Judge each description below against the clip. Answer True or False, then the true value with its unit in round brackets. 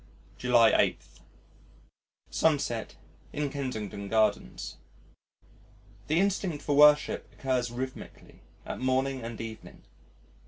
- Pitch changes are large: False (4.2 semitones)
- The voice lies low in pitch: True (130 Hz)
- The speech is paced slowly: True (90 wpm)